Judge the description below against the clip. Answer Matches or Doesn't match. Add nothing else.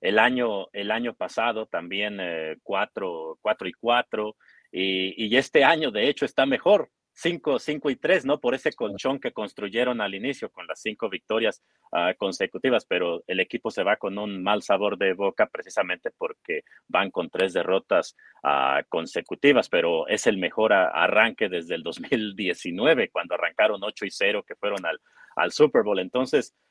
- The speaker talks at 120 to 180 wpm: Matches